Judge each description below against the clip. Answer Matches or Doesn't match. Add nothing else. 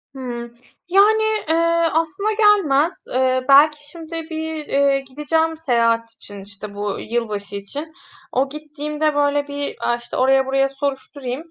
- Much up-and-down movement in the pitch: Doesn't match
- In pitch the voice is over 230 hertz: Matches